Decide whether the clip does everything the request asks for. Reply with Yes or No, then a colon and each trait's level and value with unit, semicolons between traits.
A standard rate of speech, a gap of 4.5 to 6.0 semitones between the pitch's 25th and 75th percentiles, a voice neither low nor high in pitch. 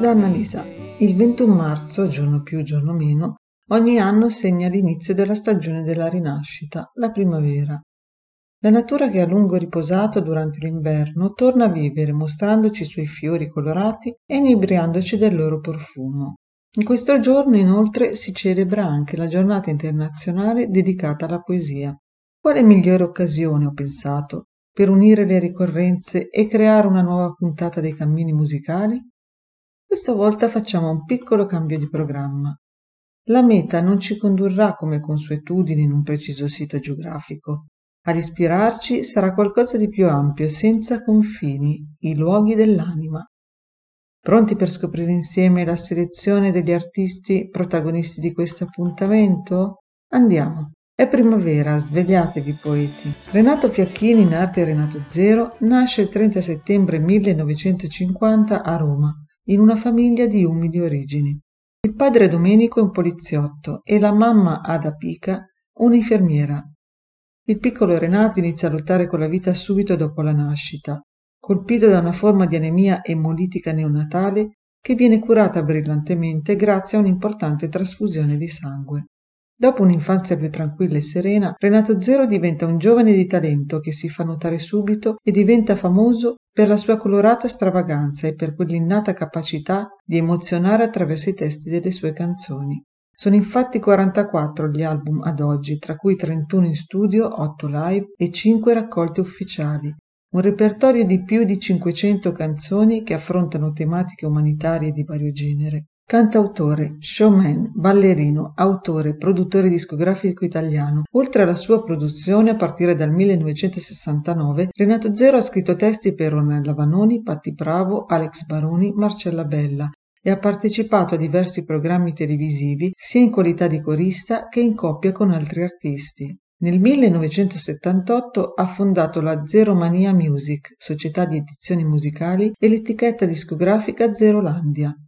Yes: average, 140 wpm; average, 4.9 semitones; medium, 180 Hz